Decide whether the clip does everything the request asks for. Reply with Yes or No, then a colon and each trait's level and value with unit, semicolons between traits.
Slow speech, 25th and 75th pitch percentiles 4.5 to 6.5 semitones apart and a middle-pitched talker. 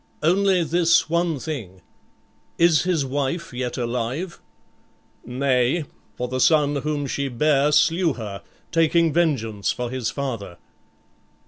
Yes: slow, 120 wpm; average, 5.1 semitones; medium, 145 Hz